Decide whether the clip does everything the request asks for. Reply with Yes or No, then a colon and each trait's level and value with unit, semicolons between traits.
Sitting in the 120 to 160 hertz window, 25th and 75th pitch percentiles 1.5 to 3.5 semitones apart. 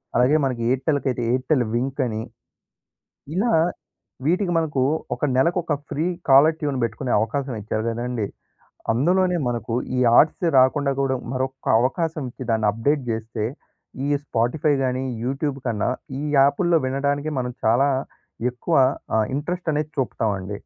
No: low, 135 Hz; average, 4.0 semitones